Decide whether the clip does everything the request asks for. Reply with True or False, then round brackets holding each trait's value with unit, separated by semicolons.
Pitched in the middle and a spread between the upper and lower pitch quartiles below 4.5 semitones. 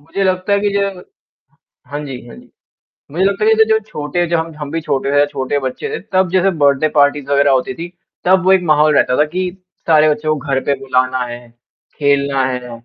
False (150 Hz; 4.8 semitones)